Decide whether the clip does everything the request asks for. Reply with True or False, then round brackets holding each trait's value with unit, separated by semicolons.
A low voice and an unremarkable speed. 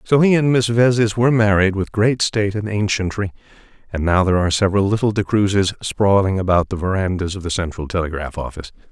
True (100 Hz; 190 wpm)